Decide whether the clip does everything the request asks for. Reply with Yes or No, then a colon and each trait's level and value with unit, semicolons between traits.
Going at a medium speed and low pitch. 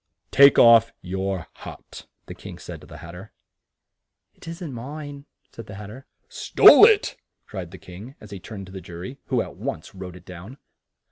Yes: average, 190 wpm; low, 105 Hz